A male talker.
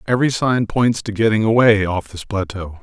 Yes: male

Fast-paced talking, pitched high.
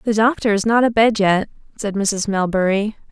No: average, 175 wpm; high, 210 Hz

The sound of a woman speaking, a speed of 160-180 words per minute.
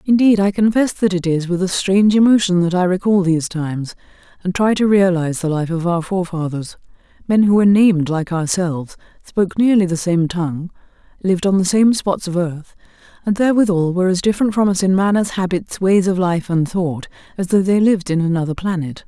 No: female; average, 200 wpm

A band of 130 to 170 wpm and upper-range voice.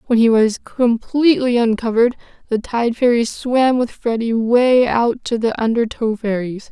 Yes: average, 150 wpm; high, 235 Hz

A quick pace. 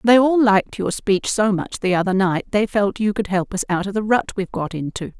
Yes: fast, 265 wpm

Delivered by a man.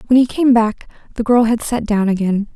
No: female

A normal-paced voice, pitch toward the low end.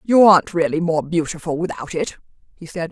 No: average, 185 wpm; medium, 170 Hz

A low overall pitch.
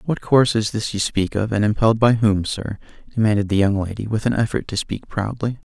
Yes: low, 110 Hz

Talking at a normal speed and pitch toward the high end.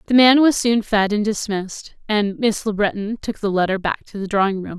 No: fast, 240 wpm; high, 210 Hz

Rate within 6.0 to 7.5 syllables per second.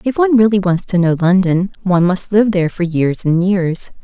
No: 5.4 syllables/s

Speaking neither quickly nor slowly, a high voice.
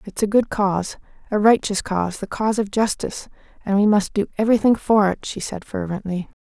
Yes: average, 180 wpm; high, 205 Hz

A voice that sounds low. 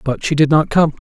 No: medium, 150 Hz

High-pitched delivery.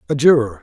No: low, 130 Hz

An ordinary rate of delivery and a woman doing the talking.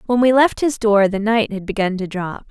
No: fast, 265 wpm; female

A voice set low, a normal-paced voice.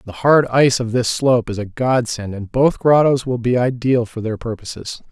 No: low, 120 Hz; fast, 210 wpm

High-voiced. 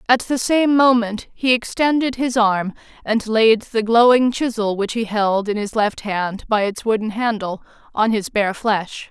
Yes: high, 225 Hz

